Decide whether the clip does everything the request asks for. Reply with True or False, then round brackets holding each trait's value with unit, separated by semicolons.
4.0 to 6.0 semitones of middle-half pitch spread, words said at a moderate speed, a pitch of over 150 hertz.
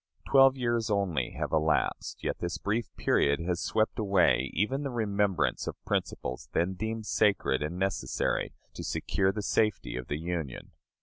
False (5.0 semitones; 160 wpm; 95 Hz)